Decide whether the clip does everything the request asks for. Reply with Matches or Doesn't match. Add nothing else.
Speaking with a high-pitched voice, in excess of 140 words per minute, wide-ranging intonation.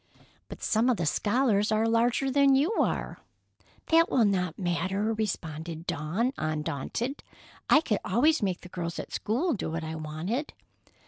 Matches